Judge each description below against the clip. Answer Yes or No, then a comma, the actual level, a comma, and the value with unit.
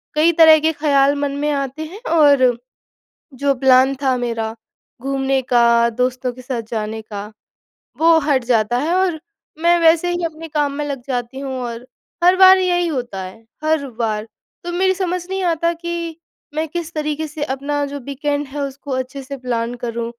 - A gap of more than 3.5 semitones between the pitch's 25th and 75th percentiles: Yes, average, 4.4 semitones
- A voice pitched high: Yes, very high, 280 Hz